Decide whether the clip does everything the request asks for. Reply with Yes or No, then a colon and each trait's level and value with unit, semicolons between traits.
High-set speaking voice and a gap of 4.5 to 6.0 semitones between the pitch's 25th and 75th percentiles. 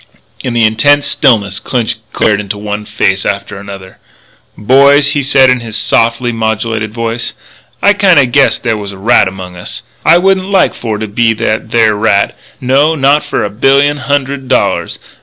No: low, 115 Hz; average, 4.8 semitones